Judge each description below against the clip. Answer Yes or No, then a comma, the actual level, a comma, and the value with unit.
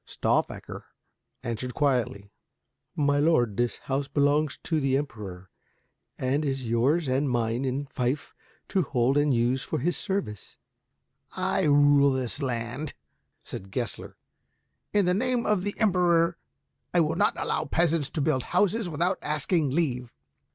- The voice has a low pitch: No, medium, 145 Hz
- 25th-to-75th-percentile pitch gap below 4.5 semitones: No, average, 4.8 semitones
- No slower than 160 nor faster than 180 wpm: No, average, 145 wpm